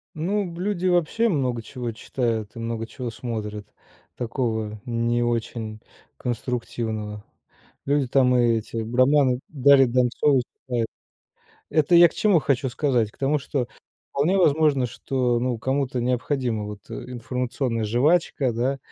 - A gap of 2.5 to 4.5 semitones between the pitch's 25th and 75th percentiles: Yes, average, 3.4 semitones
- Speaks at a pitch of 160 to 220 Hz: No, low, 125 Hz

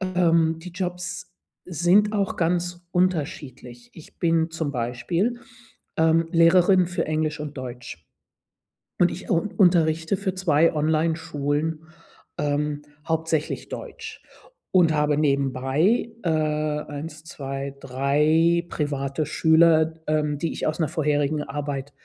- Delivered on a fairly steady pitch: No, average, 3.0 semitones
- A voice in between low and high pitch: Yes, medium, 160 Hz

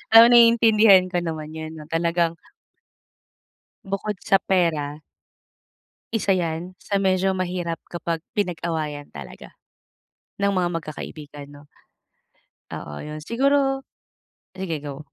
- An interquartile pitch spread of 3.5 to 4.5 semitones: Yes, average, 4.0 semitones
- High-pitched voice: No, medium, 175 Hz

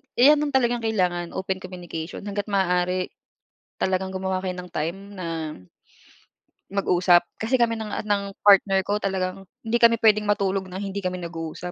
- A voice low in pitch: No, high, 190 Hz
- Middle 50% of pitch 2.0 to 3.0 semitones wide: Yes, narrow, 2.5 semitones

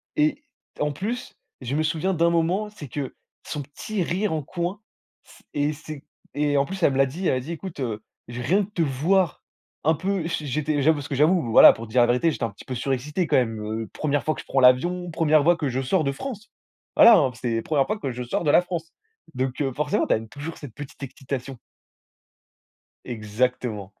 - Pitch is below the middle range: No, medium, 145 Hz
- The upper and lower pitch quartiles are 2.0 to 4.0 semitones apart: No, average, 4.9 semitones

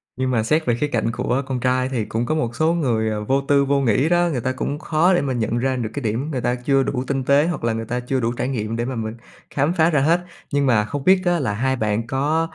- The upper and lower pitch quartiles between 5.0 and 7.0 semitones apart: No, average, 3.6 semitones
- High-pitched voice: No, low, 130 Hz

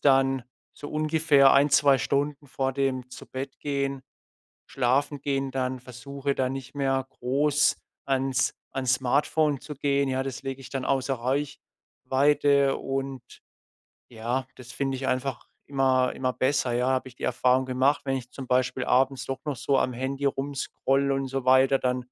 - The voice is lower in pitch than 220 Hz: Yes, low, 135 Hz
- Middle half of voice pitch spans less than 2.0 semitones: Yes, narrow, 1.2 semitones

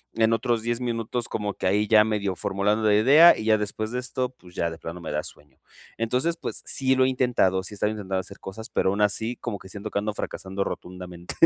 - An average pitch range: Yes, average, 3.6 semitones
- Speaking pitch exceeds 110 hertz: No, low, 105 Hz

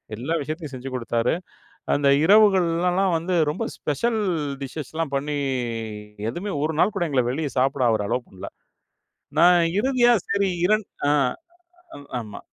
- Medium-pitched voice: Yes, medium, 160 Hz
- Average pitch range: No, wide, 6.2 semitones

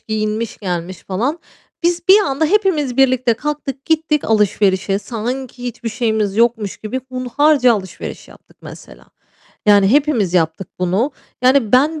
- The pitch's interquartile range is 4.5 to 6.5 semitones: Yes, average, 5.2 semitones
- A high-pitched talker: Yes, high, 240 Hz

